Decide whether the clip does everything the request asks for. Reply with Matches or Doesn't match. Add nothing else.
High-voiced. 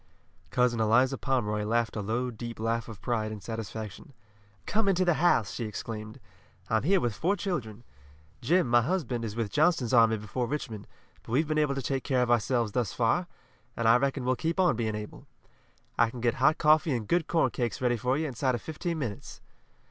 Doesn't match